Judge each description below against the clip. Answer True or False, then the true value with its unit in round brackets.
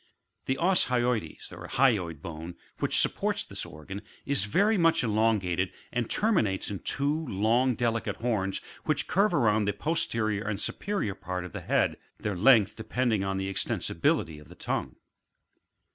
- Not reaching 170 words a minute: True (150 wpm)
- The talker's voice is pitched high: False (110 Hz)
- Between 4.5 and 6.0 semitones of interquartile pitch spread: True (5.0 semitones)